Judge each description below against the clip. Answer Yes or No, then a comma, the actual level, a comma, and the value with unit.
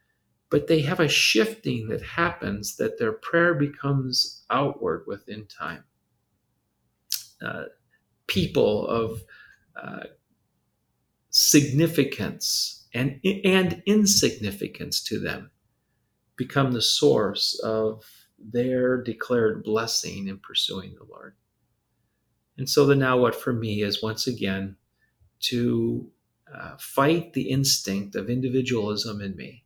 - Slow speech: Yes, slow, 110 wpm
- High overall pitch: No, low, 125 Hz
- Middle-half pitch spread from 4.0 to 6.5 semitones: Yes, average, 4.4 semitones